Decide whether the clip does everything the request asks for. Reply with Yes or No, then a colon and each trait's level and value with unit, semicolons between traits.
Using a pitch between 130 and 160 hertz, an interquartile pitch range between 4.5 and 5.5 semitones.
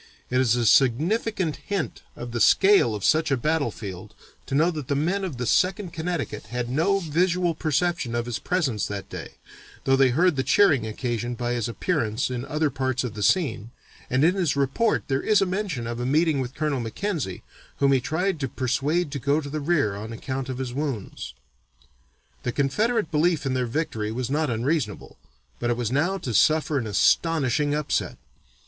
Yes: medium, 140 Hz; average, 5.2 semitones